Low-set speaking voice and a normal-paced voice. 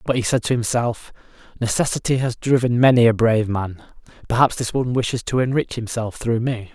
Yes: low, 120 Hz; average, 185 wpm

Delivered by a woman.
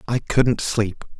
No: male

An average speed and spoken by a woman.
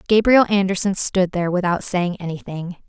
Yes: average, 145 wpm; female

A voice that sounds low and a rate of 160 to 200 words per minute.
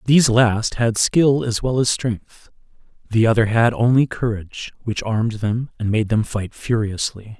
Yes: low, 115 Hz; average, 170 wpm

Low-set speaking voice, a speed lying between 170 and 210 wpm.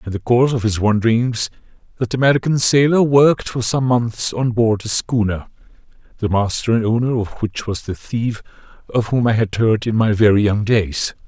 Yes: low, 115 Hz; average, 190 wpm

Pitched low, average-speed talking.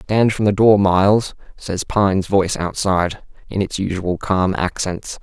Yes: very low, 95 Hz; average, 160 wpm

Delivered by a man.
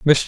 Yes: male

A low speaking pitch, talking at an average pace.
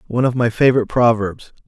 Yes: low, 115 Hz; average, 180 wpm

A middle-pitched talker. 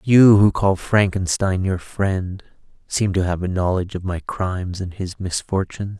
No: very low, 95 Hz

